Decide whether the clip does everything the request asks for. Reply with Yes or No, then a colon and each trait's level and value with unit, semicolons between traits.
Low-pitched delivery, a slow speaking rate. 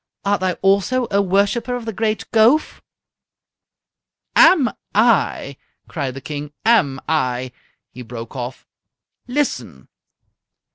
No: high, 195 Hz; slow, 110 wpm